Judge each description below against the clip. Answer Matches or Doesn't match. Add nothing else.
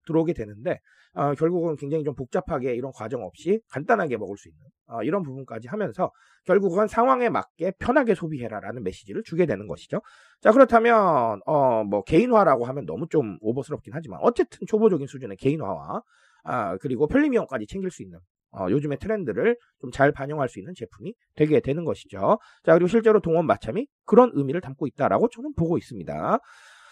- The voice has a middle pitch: Matches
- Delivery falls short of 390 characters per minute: Doesn't match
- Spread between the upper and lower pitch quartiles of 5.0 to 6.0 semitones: Doesn't match